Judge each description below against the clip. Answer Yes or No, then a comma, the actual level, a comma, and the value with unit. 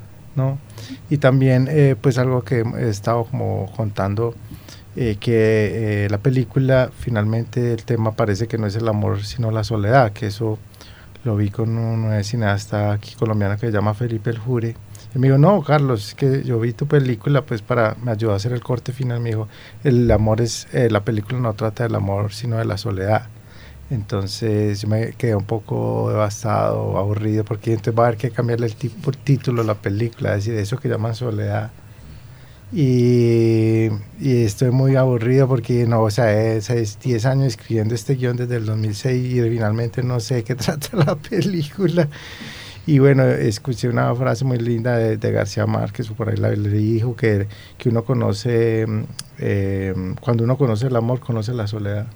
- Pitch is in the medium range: No, low, 115 Hz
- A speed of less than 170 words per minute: No, average, 185 wpm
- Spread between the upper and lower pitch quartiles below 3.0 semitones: Yes, narrow, 2.6 semitones